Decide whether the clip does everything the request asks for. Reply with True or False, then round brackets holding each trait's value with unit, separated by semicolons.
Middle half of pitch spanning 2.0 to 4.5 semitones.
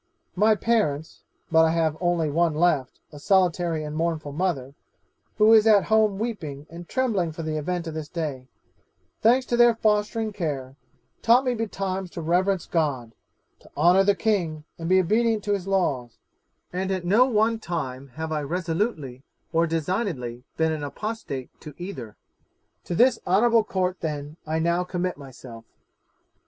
False (5.2 semitones)